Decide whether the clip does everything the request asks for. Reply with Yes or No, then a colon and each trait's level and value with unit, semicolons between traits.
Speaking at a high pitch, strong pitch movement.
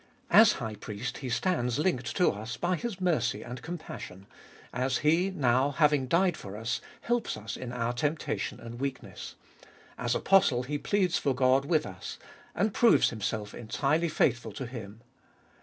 No: low, 130 Hz; wide, 6.2 semitones